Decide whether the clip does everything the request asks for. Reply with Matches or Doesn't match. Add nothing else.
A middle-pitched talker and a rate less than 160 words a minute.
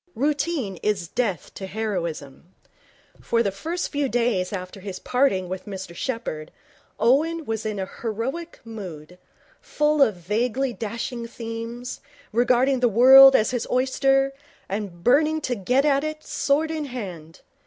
Doesn't match